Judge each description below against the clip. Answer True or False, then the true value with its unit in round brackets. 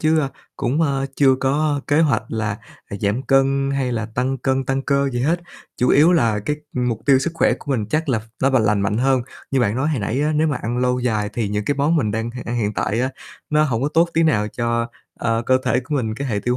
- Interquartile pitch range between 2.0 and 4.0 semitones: True (3.7 semitones)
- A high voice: False (130 Hz)